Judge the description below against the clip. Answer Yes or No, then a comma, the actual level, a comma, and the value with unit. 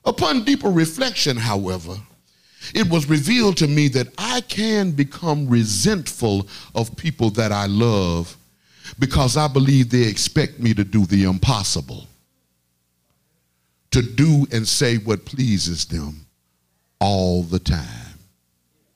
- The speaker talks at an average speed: No, slow, 125 wpm